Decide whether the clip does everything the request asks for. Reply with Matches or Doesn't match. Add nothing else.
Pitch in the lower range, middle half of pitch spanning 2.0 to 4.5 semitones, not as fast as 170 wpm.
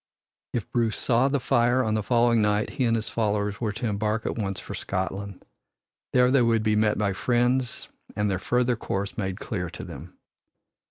Doesn't match